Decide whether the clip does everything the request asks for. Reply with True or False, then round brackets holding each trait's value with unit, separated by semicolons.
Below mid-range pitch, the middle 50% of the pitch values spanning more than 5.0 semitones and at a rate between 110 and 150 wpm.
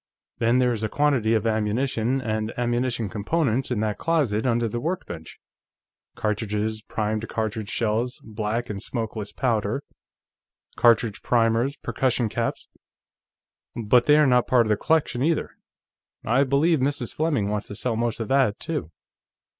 False (115 Hz; 3.2 semitones; 145 wpm)